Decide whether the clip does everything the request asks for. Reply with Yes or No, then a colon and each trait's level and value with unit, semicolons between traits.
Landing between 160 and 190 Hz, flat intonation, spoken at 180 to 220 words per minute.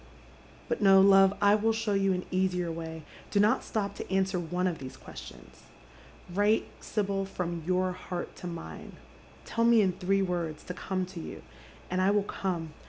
Yes: medium, 185 Hz; narrow, 2.1 semitones; average, 185 wpm